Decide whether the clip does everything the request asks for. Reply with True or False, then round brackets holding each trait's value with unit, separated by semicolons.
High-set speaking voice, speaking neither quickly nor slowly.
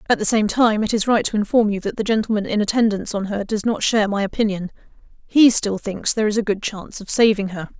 False (210 Hz; 255 wpm)